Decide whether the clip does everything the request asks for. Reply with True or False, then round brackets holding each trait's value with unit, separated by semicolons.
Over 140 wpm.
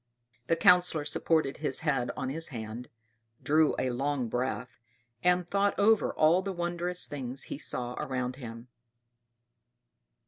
False (135 wpm)